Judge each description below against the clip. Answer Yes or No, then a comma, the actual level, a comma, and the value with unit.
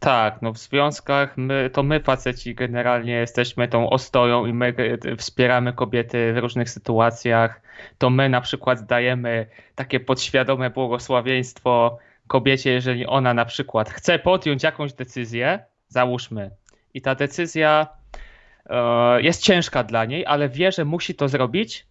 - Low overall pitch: Yes, low, 125 Hz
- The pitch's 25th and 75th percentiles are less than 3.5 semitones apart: Yes, average, 2.8 semitones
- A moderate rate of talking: Yes, average, 140 wpm